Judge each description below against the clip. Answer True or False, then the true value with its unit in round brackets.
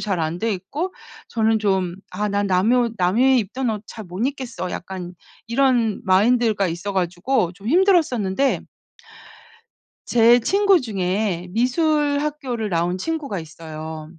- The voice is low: False (215 Hz)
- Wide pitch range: True (5.8 semitones)